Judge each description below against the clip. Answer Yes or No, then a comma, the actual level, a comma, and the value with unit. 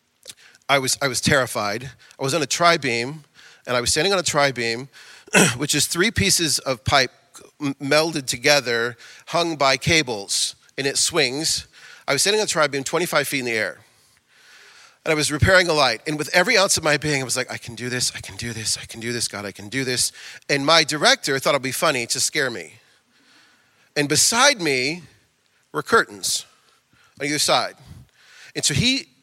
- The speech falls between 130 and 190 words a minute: No, average, 200 wpm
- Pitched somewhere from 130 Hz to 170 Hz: Yes, medium, 140 Hz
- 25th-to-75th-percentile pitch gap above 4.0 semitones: Yes, average, 4.4 semitones